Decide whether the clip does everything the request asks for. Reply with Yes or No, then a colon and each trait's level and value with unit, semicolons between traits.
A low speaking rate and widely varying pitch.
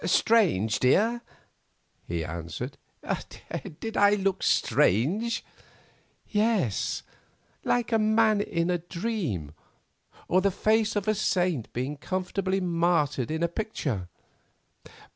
Yes: slow, 105 wpm; wide, 7.5 semitones